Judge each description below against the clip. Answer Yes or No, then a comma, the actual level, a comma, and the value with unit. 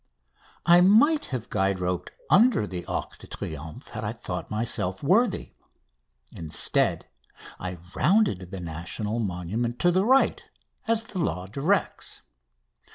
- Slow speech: Yes, slow, 130 wpm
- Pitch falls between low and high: No, low, 115 Hz